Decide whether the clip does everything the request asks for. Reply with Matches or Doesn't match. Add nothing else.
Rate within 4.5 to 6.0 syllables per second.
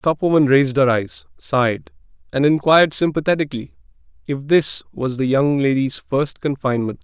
Matches